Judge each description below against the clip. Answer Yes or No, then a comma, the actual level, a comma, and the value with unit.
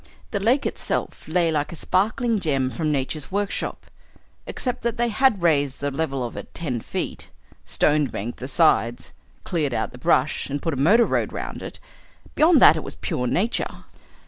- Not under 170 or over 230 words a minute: Yes, average, 180 wpm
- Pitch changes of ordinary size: No, wide, 7.0 semitones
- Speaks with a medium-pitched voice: Yes, medium, 155 Hz